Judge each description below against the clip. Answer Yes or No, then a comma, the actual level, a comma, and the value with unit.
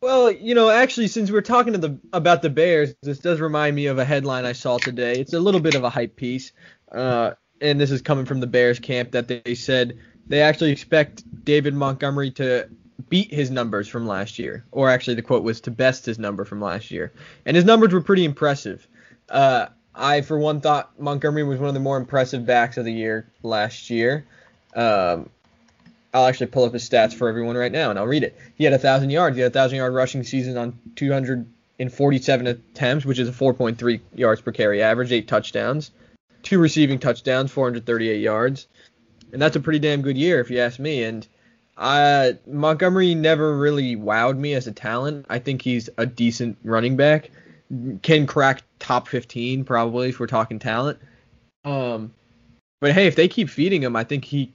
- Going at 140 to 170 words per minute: No, average, 200 wpm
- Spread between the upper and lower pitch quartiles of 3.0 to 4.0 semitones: Yes, average, 3.6 semitones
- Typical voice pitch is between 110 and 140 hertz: Yes, low, 130 Hz